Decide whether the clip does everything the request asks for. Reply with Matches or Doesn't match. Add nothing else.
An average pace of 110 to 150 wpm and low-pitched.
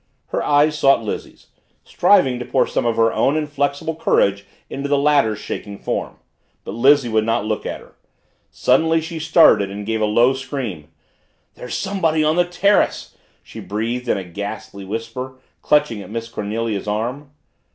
Doesn't match